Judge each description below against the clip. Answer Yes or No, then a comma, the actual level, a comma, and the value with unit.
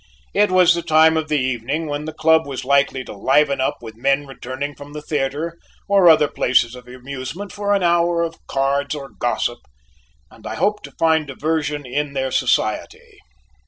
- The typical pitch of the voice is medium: Yes, medium, 150 Hz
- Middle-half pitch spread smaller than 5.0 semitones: Yes, average, 3.4 semitones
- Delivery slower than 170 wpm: No, average, 185 wpm